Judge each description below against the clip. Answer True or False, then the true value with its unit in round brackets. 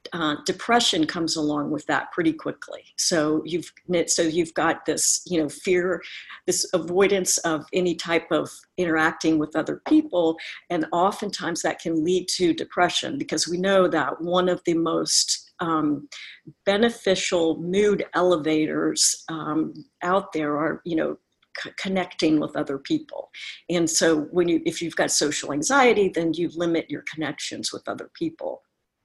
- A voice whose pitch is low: False (170 Hz)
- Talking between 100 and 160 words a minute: True (155 wpm)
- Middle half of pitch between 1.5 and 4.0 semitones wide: True (2.7 semitones)